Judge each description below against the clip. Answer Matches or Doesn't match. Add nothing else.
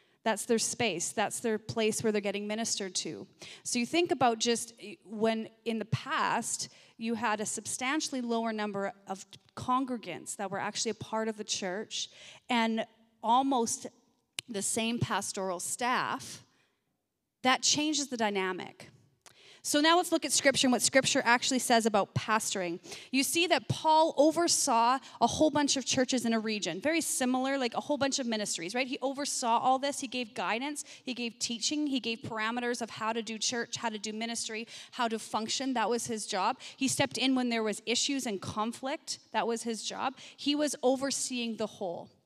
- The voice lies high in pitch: Matches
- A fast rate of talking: Doesn't match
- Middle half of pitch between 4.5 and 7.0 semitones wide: Doesn't match